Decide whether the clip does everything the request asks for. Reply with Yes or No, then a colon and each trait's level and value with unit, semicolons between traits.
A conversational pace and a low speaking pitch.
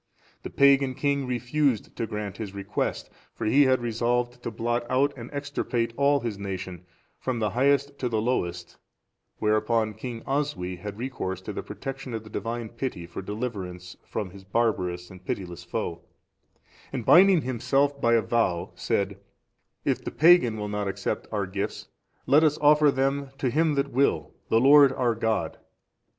Yes: average, 165 wpm; low, 115 Hz